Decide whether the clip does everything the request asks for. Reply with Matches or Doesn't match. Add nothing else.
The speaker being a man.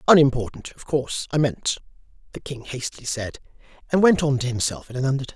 Matches